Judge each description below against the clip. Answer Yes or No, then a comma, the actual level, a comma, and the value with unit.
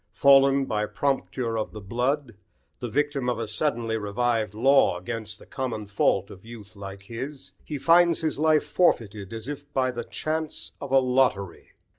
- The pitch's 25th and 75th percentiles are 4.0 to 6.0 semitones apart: Yes, average, 4.5 semitones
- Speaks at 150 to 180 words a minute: Yes, average, 170 wpm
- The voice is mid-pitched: No, low, 125 Hz